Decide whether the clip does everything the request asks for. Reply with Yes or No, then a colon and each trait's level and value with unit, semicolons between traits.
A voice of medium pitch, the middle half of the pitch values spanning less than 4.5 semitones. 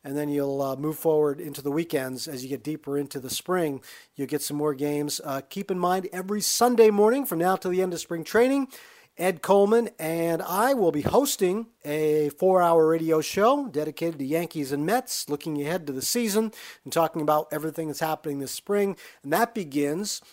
No: medium, 160 Hz; average, 5.1 semitones